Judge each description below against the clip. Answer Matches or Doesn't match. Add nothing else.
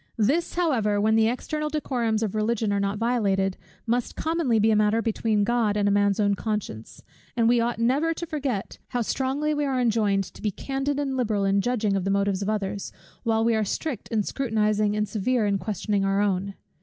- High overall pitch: Matches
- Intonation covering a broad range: Doesn't match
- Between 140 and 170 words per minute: Doesn't match